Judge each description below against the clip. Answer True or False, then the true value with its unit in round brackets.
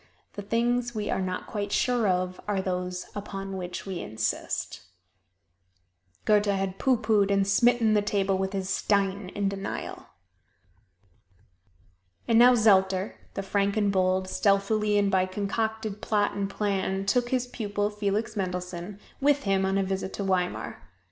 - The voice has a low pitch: False (200 Hz)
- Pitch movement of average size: False (1.9 semitones)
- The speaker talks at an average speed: True (150 wpm)